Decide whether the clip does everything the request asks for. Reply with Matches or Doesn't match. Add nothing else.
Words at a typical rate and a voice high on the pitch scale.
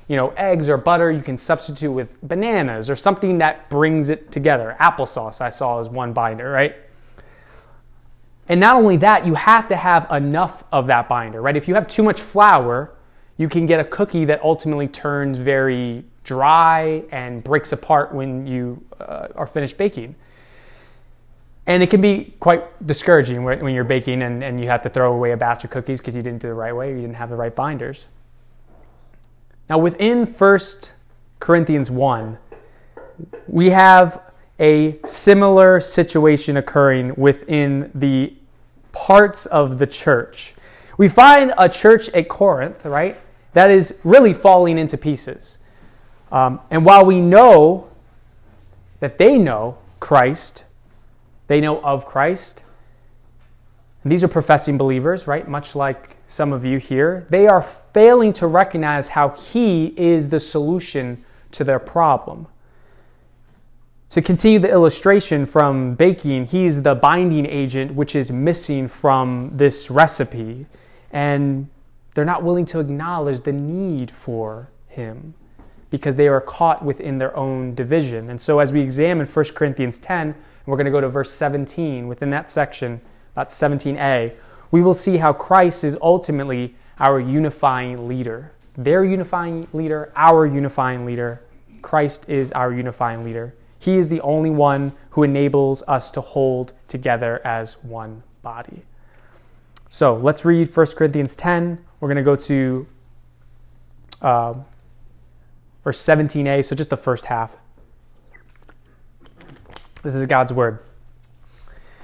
Doesn't match